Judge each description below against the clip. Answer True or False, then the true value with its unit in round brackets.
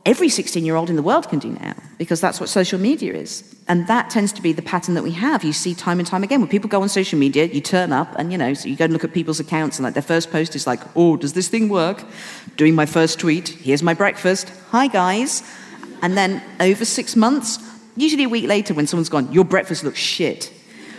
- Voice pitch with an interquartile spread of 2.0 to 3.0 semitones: False (4.5 semitones)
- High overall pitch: False (180 Hz)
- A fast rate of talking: True (255 wpm)